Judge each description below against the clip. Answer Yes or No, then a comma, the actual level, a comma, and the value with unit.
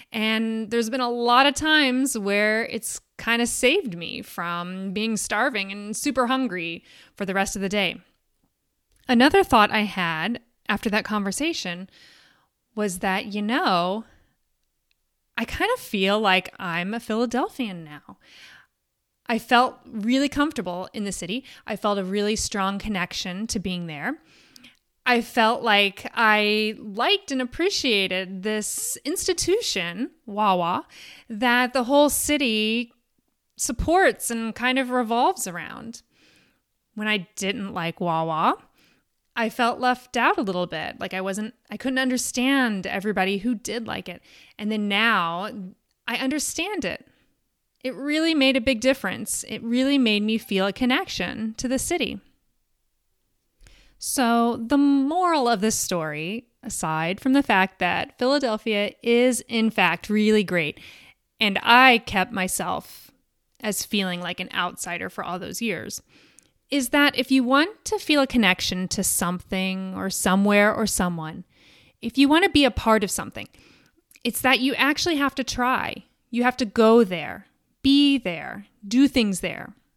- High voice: Yes, high, 225 Hz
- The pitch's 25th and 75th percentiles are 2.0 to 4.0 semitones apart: No, average, 4.7 semitones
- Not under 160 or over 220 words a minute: No, average, 150 wpm